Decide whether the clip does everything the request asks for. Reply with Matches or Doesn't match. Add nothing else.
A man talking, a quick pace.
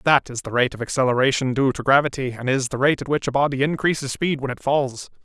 Matches